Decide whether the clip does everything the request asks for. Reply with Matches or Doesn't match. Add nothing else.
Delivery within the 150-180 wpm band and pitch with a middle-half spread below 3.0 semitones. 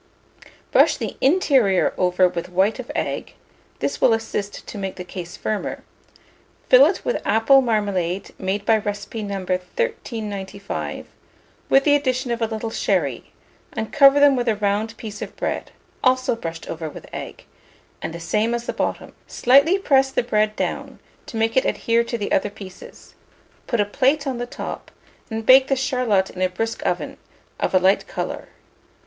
Doesn't match